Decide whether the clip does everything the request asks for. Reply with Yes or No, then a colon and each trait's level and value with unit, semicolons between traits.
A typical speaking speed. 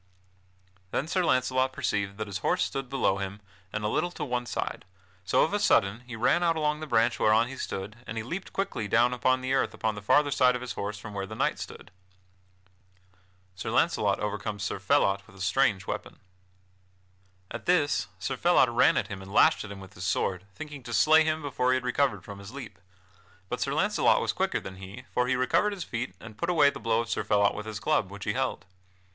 No: fast, 225 wpm